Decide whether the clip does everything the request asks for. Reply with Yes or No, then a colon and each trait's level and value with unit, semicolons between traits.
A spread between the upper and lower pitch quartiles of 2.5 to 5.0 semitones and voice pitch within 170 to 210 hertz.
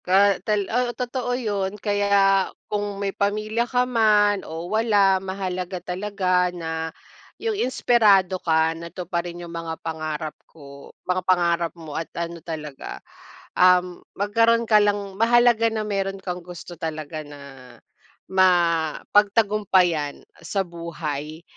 Yes: average, 3.6 semitones; medium, 185 Hz